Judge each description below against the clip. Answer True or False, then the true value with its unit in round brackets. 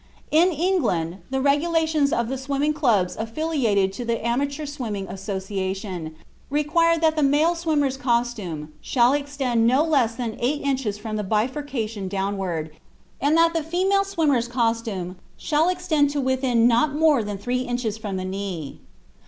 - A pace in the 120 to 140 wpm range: False (150 wpm)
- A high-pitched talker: True (250 Hz)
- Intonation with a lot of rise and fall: True (6.1 semitones)